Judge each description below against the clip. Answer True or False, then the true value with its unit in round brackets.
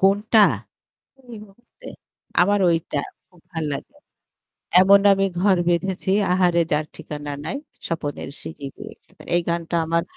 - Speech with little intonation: False (3.4 semitones)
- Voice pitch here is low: False (175 Hz)